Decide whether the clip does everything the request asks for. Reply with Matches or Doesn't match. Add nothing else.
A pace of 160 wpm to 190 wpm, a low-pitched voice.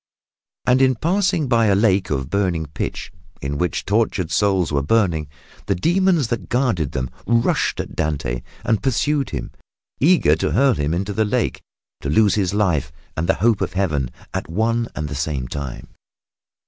Matches